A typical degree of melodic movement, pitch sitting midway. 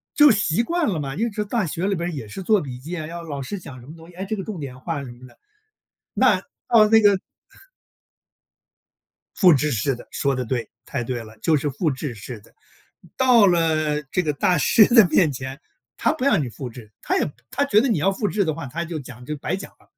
No: wide, 6.9 semitones; medium, 160 Hz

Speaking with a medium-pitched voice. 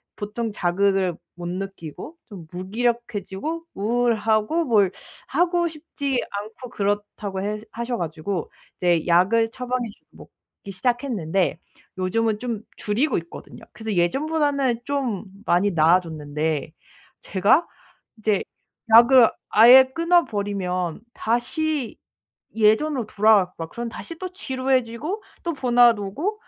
No: high, 220 Hz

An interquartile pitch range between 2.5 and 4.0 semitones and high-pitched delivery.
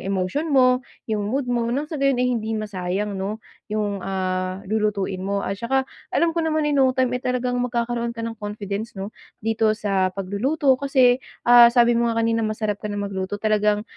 Yes: average, 3.7 semitones; high, 225 Hz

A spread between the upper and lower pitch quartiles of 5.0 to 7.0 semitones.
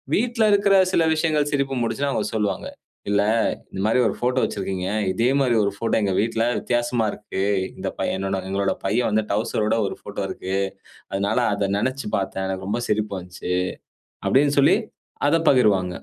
Yes: wide, 5.4 semitones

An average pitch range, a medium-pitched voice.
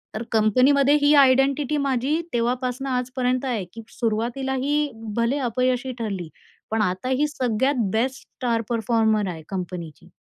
No: average, 3.4 semitones; very high, 250 Hz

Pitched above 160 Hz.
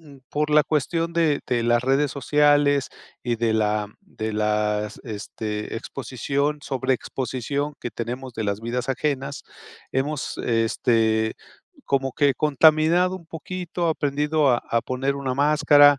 No: low, 135 Hz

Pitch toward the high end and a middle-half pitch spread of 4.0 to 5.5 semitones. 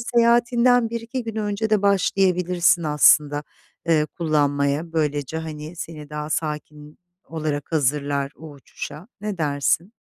No: medium, 160 Hz; average, 5.2 semitones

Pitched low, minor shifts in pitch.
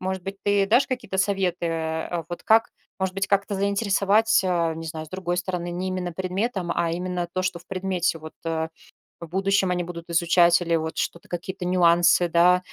No: medium, 180 Hz; narrow, 2.1 semitones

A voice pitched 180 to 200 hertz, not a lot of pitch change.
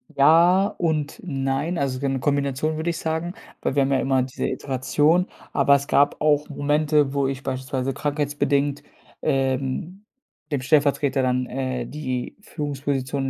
No: medium, 140 Hz; narrow, 2.2 semitones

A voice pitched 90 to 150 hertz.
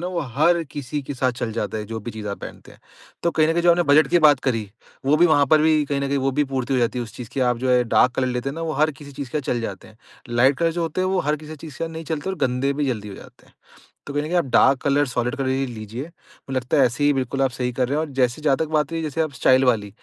Yes: medium, 140 Hz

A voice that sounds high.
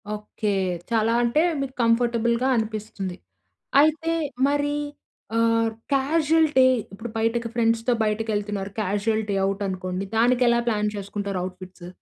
Yes: high, 225 Hz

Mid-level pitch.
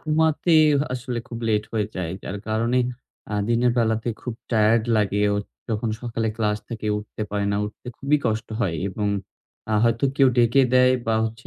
No: low, 115 Hz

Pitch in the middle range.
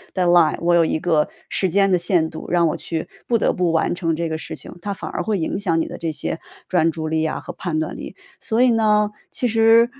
Yes: medium, 175 Hz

